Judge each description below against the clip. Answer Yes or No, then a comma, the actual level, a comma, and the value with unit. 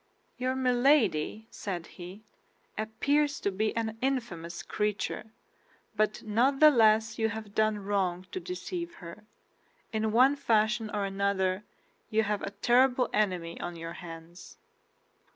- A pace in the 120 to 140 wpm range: Yes, slow, 135 wpm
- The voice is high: Yes, high, 215 Hz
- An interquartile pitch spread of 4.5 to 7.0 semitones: No, average, 3.9 semitones